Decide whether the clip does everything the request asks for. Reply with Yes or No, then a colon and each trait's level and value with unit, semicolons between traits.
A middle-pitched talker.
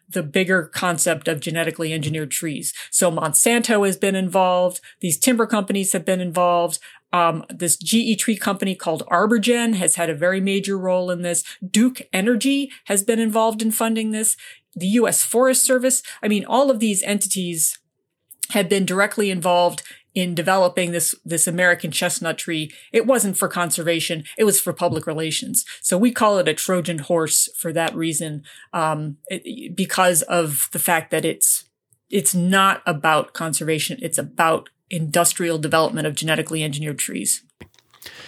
Yes: medium, 180 Hz